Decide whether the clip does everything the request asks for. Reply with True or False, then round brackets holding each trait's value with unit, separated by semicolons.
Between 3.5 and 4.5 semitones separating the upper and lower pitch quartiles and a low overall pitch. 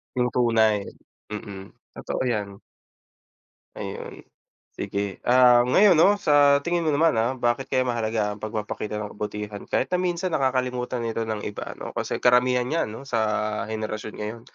True (4.0 semitones; 120 Hz)